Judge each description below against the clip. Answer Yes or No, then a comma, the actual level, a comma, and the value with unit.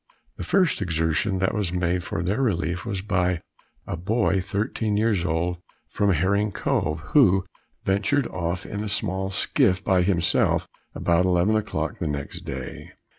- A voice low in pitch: Yes, very low, 95 Hz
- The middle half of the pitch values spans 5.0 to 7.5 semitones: No, average, 2.9 semitones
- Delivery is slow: No, average, 155 wpm